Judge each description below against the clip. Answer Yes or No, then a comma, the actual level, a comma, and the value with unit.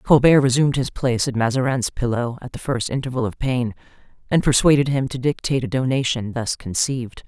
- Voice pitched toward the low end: Yes, low, 125 Hz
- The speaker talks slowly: No, average, 180 wpm